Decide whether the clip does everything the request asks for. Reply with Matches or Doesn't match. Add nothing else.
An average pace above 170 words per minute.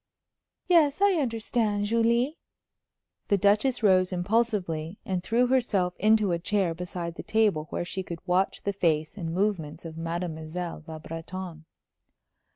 Doesn't match